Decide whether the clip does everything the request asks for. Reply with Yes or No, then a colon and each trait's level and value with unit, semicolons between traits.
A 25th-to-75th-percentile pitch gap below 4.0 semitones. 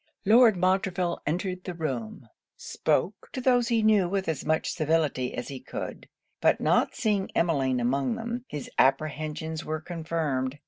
No: average, 4.8 semitones